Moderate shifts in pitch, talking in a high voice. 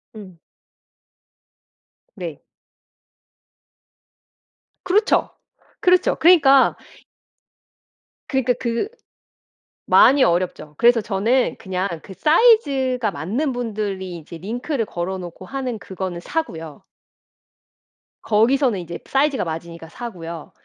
No: wide, 6.8 semitones; high, 220 Hz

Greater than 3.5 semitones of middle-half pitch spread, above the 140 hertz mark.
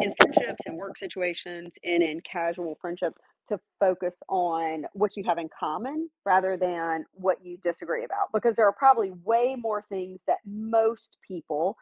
Yes: average, 3.9 semitones; medium, 185 Hz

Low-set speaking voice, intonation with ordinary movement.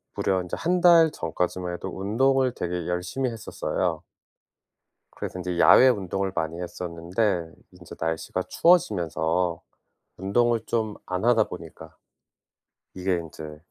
Yes: very low, 90 Hz; average, 5.0 semitones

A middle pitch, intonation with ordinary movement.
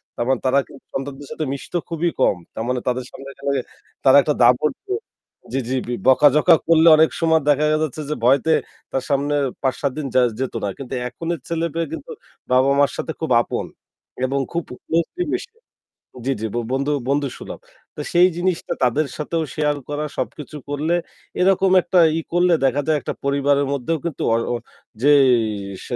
Yes: medium, 145 Hz; average, 3.3 semitones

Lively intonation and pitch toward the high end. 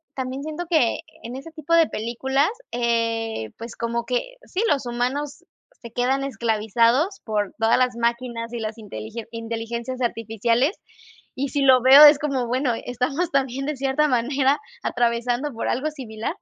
No: average, 3.2 semitones; high, 245 Hz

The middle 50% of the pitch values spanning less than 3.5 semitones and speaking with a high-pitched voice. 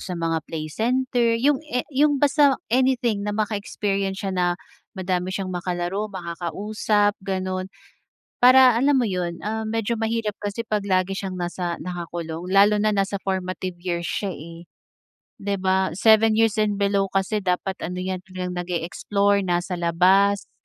Yes: average, 3.0 semitones; high, 195 Hz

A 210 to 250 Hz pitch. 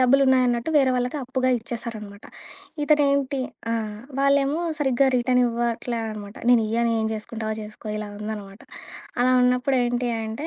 Yes: high, 245 Hz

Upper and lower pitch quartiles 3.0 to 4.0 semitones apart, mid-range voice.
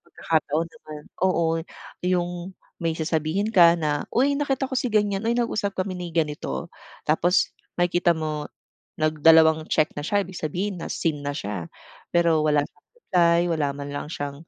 Yes: average, 3.6 semitones; medium, 165 Hz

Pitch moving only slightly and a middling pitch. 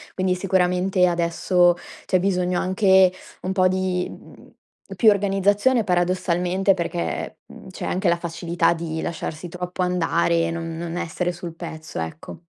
Yes: narrow, 1.7 semitones; medium, 180 Hz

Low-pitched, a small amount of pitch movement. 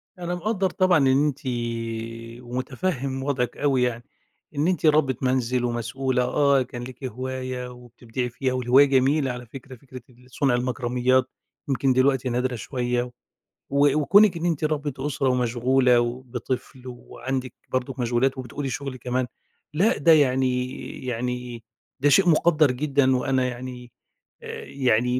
Yes: low, 130 Hz; narrow, 2.1 semitones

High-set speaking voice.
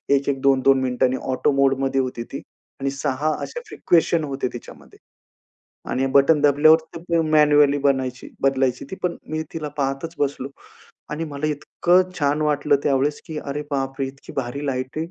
No: medium, 140 Hz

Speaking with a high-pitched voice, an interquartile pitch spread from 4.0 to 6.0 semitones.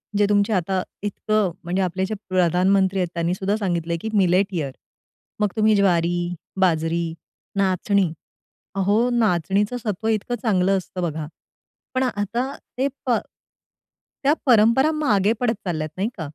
No: high, 195 Hz; average, 3.3 semitones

